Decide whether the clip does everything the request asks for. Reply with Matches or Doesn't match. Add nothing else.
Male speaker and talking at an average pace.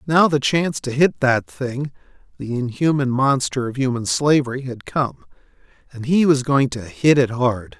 Matches